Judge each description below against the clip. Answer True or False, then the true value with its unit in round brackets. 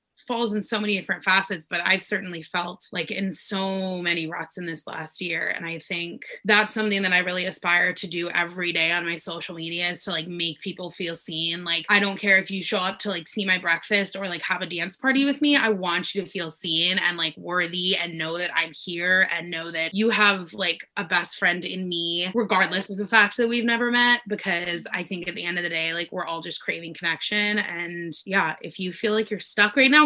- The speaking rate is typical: False (245 wpm)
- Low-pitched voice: False (180 Hz)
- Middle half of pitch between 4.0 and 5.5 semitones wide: False (3.0 semitones)